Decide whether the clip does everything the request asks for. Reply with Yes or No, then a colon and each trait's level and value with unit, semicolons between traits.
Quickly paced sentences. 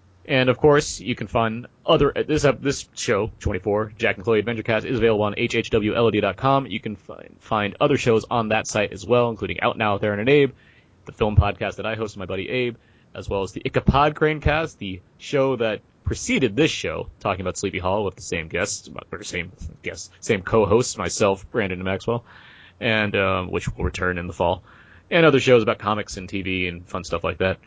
Yes: fast, 215 wpm